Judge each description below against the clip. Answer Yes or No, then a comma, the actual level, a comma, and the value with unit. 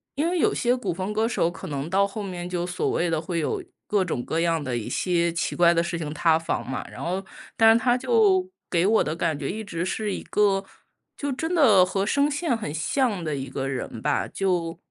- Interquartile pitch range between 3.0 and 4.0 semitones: No, average, 5.2 semitones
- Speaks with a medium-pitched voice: Yes, medium, 180 Hz